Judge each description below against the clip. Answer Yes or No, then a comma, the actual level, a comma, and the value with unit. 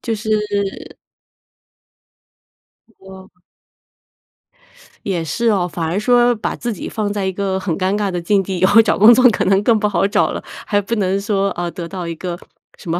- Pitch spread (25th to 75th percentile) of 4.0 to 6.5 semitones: No, narrow, 2.6 semitones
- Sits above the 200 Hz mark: No, high, 195 Hz